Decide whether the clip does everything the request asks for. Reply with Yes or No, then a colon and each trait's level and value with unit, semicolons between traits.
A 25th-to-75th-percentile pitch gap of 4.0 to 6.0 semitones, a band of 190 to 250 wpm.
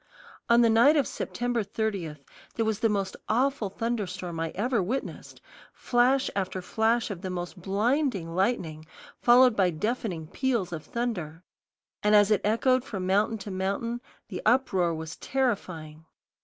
No: average, 4.8 semitones; average, 150 wpm